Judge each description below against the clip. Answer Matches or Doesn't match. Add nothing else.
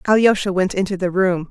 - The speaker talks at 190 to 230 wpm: Matches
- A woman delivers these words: Matches